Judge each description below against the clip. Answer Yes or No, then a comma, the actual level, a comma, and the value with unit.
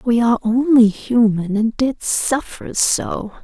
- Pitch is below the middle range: No, high, 230 Hz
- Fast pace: No, average, 140 wpm